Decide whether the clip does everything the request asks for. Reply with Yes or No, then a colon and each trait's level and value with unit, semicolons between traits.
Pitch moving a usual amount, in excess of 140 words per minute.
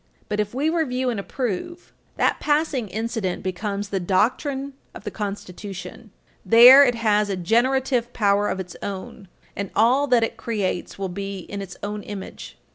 Yes: average, 4.1 semitones; average, 165 wpm